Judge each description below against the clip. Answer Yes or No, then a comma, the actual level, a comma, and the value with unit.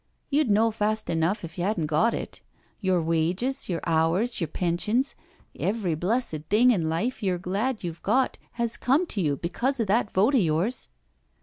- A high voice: Yes, high, 200 Hz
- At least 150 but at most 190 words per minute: Yes, average, 180 wpm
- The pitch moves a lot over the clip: Yes, wide, 5.8 semitones